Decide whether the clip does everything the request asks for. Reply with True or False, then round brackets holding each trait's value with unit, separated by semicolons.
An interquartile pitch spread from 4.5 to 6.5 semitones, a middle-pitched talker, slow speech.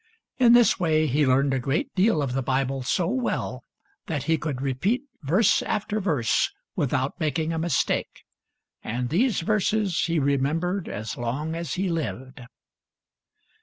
False (5.4 semitones; 155 Hz; 150 wpm)